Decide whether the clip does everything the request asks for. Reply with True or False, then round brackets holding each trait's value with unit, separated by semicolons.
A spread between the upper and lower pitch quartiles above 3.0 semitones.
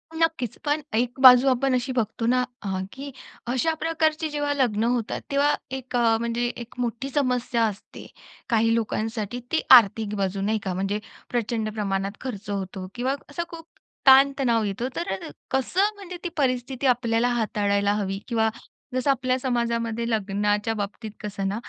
True (3.8 semitones)